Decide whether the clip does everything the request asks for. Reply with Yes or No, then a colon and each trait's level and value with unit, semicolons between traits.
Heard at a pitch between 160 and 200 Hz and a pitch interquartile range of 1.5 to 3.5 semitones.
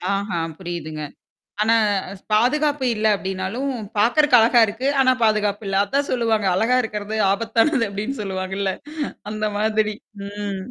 No: high, 215 Hz; average, 3.2 semitones